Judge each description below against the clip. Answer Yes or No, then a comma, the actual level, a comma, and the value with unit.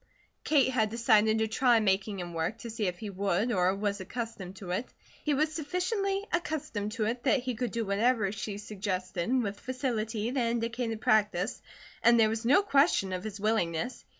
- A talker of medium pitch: No, high, 220 Hz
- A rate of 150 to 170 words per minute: No, average, 185 wpm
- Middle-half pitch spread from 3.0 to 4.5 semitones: Yes, average, 3.8 semitones